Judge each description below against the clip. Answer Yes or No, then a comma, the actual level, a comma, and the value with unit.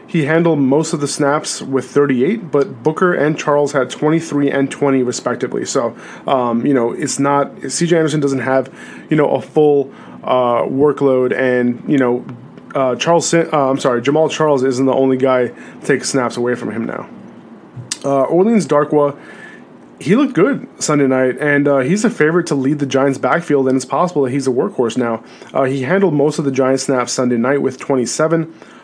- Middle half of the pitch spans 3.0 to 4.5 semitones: No, narrow, 2.5 semitones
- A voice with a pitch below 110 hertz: No, medium, 140 Hz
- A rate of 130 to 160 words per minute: No, average, 190 wpm